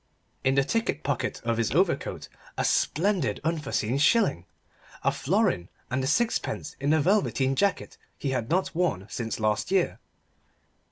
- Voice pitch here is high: No, medium, 140 Hz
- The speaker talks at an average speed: Yes, average, 150 wpm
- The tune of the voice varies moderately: No, wide, 7.4 semitones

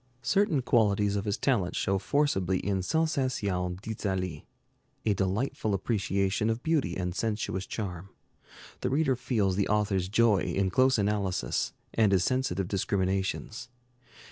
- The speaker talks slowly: Yes, slow, 130 wpm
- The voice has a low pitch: Yes, low, 100 Hz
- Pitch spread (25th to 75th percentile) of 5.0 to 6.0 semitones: No, average, 3.9 semitones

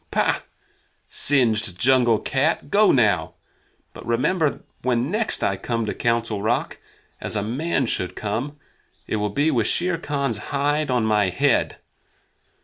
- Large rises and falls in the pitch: No, average, 5.0 semitones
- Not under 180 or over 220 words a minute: No, average, 145 wpm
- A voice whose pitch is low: Yes, low, 120 Hz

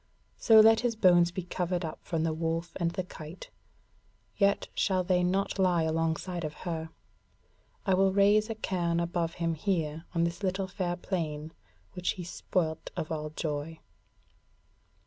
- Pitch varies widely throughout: No, narrow, 2.5 semitones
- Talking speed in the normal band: Yes, average, 160 wpm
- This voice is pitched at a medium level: Yes, medium, 175 Hz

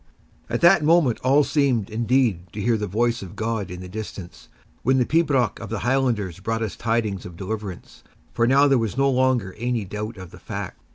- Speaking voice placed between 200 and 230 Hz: No, low, 115 Hz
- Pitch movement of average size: Yes, average, 4.4 semitones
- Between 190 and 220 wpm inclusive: Yes, fast, 205 wpm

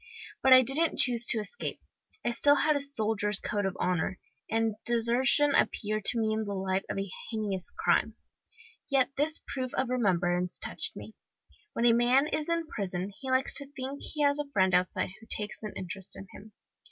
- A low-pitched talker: No, high, 230 Hz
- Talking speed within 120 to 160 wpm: No, average, 190 wpm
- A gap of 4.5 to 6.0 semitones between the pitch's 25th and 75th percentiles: Yes, wide, 5.4 semitones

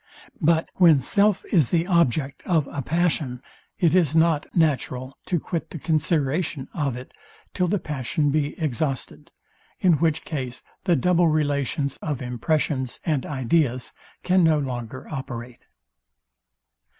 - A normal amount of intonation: Yes, average, 4.1 semitones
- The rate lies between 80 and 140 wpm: Yes, slow, 135 wpm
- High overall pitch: No, medium, 150 Hz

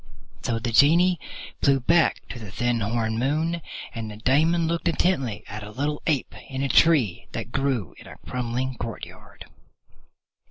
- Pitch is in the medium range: No, low, 130 Hz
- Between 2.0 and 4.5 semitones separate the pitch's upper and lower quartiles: No, wide, 5.5 semitones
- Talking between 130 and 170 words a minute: Yes, average, 160 wpm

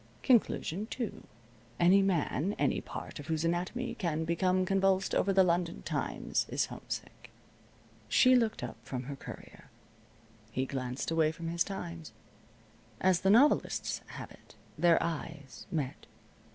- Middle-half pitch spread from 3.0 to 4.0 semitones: Yes, average, 3.5 semitones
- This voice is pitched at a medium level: Yes, medium, 175 Hz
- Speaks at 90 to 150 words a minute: Yes, average, 140 wpm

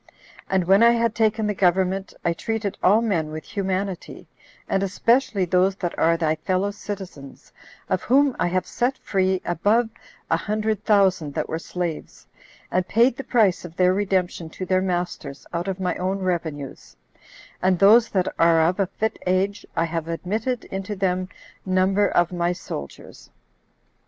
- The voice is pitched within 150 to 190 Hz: Yes, medium, 185 Hz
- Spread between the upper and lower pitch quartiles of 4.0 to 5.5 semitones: No, average, 2.8 semitones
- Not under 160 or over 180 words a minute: Yes, average, 165 wpm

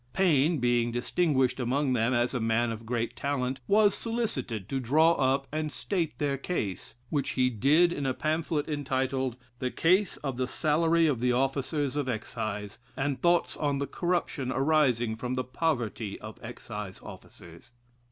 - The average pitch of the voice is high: No, low, 135 Hz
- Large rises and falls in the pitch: No, average, 4.1 semitones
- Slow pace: No, average, 160 wpm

